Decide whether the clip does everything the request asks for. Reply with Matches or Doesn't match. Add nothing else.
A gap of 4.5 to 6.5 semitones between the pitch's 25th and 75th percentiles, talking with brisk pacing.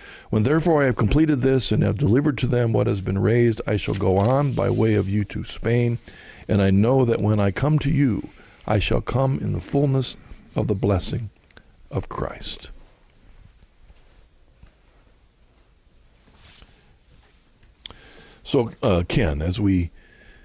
Doesn't match